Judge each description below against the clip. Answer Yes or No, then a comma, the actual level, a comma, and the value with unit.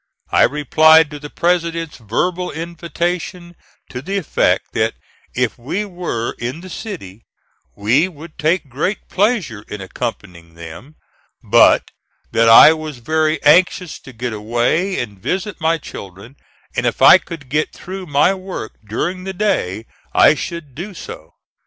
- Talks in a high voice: No, medium, 155 Hz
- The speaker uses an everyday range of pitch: No, wide, 6.9 semitones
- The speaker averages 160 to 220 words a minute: No, average, 145 wpm